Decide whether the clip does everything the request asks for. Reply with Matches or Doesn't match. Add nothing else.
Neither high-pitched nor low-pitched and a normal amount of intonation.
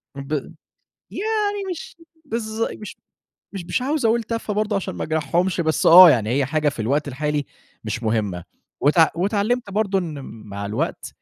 Doesn't match